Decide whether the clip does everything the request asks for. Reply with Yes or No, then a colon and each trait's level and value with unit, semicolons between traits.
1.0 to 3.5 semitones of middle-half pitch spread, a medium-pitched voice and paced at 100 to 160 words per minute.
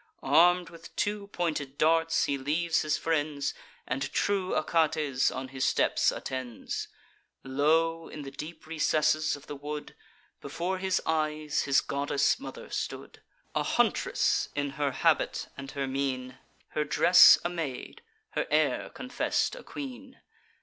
Yes: average, 3.1 semitones; medium, 150 Hz; average, 140 wpm